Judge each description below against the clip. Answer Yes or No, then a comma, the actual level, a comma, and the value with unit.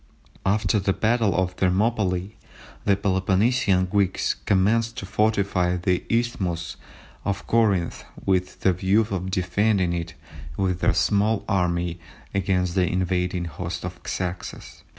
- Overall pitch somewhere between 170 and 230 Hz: No, very low, 95 Hz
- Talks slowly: Yes, slow, 125 wpm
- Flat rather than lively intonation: Yes, narrow, 2.3 semitones